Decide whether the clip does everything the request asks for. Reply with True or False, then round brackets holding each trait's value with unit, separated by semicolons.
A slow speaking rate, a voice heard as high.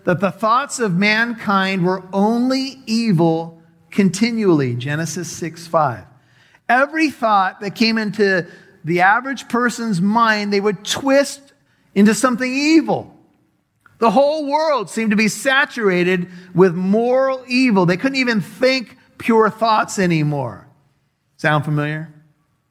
True (120 wpm; 205 Hz)